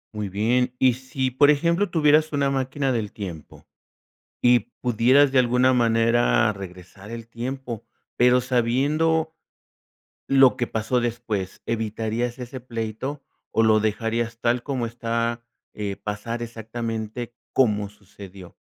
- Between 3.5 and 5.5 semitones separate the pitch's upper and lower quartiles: No, average, 2.8 semitones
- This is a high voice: No, low, 120 Hz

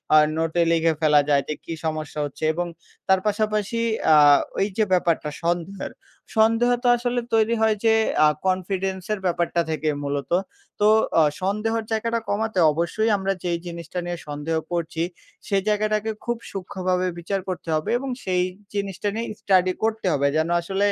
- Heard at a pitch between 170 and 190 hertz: Yes, medium, 185 Hz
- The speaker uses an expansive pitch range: No, average, 4.2 semitones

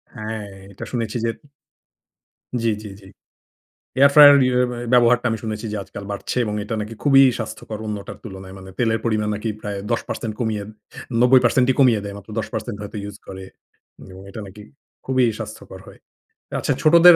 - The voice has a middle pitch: No, low, 110 Hz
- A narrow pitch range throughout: No, average, 3.2 semitones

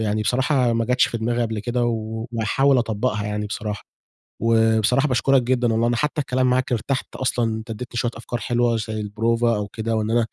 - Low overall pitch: Yes, low, 115 Hz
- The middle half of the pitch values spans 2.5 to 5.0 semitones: No, narrow, 2.1 semitones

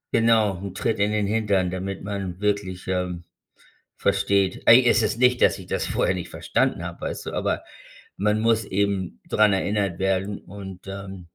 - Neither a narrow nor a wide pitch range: No, narrow, 2.2 semitones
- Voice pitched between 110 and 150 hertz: No, low, 100 Hz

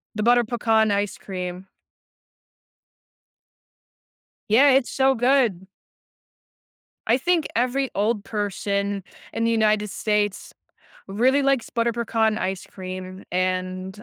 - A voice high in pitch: Yes, high, 215 Hz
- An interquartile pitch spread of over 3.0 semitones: Yes, average, 3.8 semitones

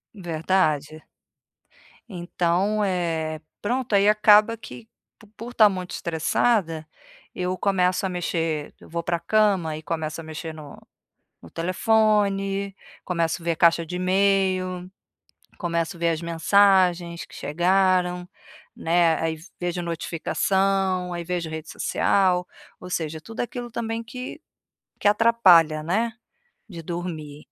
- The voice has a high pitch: No, medium, 180 Hz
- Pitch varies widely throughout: No, average, 3.2 semitones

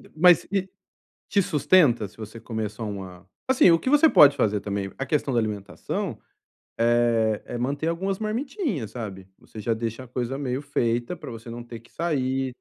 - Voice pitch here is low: Yes, low, 120 Hz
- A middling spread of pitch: No, wide, 5.7 semitones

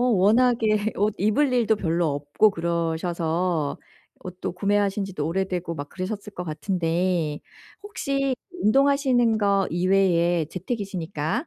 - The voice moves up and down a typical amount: Yes, average, 4.3 semitones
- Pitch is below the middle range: No, high, 190 Hz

